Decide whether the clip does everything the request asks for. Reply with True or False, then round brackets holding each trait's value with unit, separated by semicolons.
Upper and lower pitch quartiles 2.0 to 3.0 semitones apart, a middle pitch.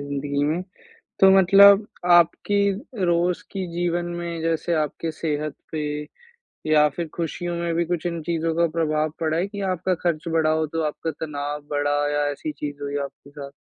True (2.6 semitones; 165 Hz)